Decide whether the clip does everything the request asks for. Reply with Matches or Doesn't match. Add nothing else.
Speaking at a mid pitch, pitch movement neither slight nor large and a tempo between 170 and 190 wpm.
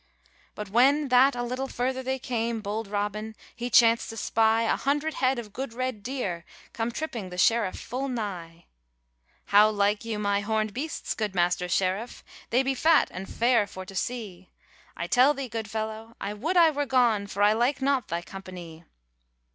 Doesn't match